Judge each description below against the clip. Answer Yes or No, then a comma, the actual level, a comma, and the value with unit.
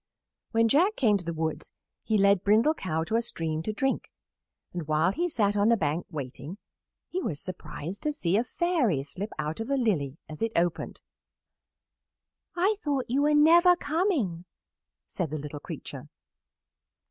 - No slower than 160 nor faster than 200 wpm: Yes, average, 170 wpm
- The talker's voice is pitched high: Yes, high, 205 Hz